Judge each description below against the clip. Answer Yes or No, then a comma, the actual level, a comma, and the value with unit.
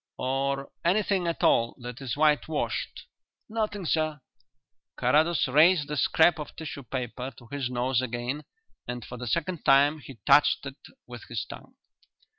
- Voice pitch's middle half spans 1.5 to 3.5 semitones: No, average, 3.9 semitones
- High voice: No, medium, 140 Hz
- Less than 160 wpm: Yes, average, 150 wpm